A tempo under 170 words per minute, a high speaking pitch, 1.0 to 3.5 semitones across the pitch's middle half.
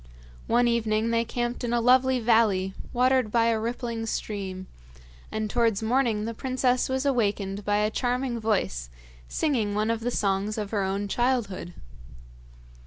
Yes: average, 155 wpm; high, 225 Hz; average, 2.9 semitones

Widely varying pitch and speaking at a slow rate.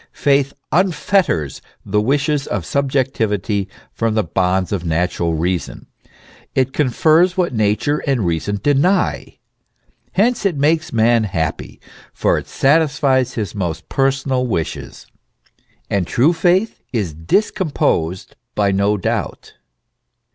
Yes: wide, 7.4 semitones; slow, 115 wpm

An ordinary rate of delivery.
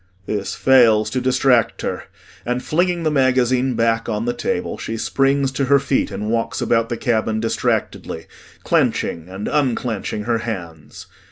Yes: average, 155 wpm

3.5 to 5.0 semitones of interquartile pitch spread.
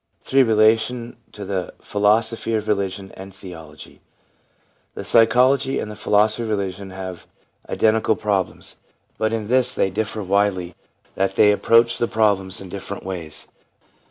No: narrow, 2.6 semitones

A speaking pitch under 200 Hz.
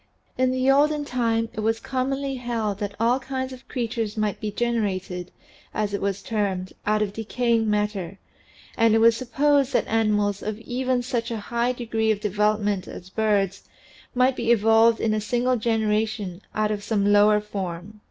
No: high, 220 Hz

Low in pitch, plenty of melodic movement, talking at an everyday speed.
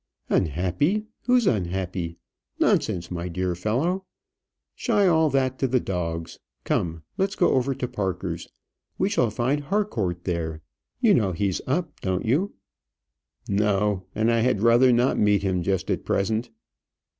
Yes: low, 105 Hz; wide, 7.0 semitones; average, 145 wpm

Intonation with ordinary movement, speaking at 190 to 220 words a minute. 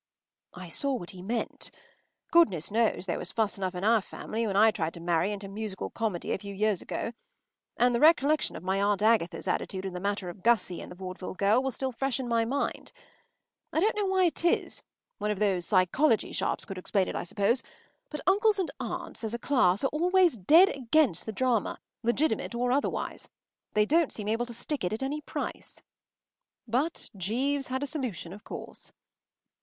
No: wide, 5.9 semitones; average, 195 wpm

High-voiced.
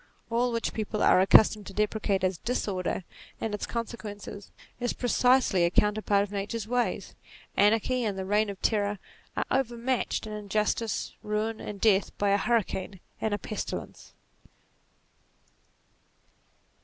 Yes: high, 210 Hz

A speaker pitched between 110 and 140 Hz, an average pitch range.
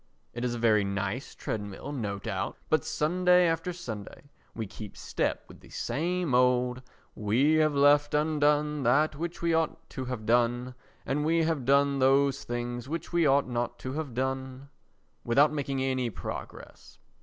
Yes: low, 135 Hz; average, 3.8 semitones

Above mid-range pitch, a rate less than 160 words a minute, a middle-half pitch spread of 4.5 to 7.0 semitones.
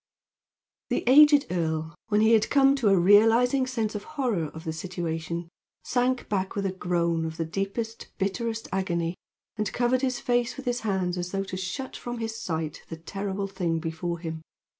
No: high, 195 Hz; average, 185 wpm; wide, 5.6 semitones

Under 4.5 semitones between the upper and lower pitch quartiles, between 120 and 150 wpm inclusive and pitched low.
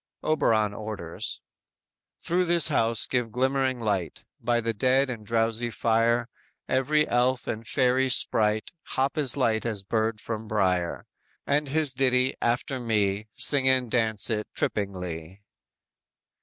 Yes: average, 3.4 semitones; slow, 135 wpm; low, 115 Hz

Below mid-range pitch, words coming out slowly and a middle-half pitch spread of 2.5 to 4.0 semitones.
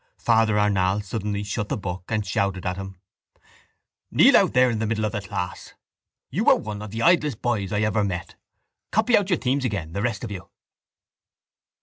No: low, 105 Hz; average, 195 wpm; average, 2.8 semitones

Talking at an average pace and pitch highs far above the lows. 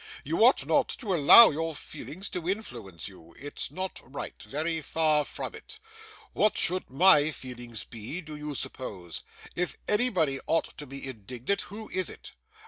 Yes: average, 160 wpm; wide, 6.3 semitones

